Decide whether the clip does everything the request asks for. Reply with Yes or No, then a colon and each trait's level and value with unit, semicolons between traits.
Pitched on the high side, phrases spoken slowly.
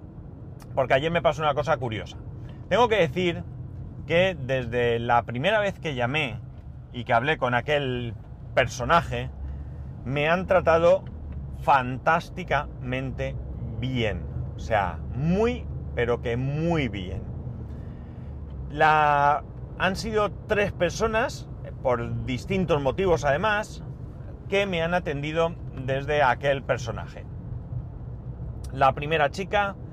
No: low, 135 Hz; slow, 110 wpm